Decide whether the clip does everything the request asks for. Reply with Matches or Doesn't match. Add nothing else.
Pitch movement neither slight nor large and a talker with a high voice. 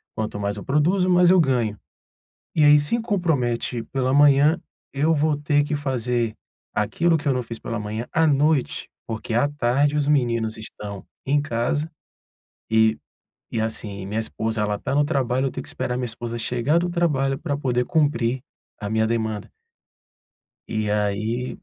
Doesn't match